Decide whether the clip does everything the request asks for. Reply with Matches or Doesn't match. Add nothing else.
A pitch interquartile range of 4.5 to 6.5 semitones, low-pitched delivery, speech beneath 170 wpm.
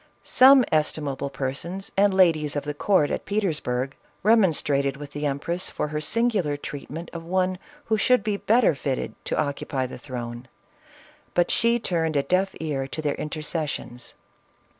Doesn't match